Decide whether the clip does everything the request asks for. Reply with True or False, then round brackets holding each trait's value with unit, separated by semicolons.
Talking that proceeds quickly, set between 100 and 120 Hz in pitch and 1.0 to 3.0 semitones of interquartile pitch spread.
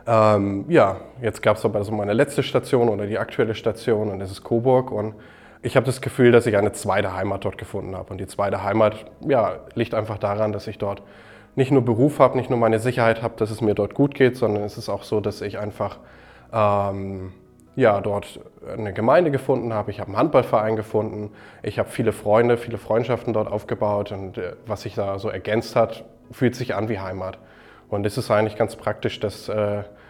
True (210 wpm; 110 Hz; 2.4 semitones)